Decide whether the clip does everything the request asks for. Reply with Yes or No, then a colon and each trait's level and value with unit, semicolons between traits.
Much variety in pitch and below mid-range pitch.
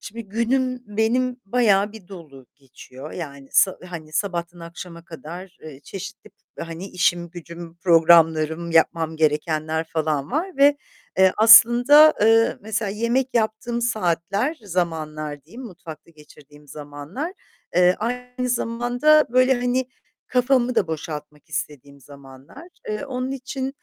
No: wide, 7.3 semitones; medium, 185 Hz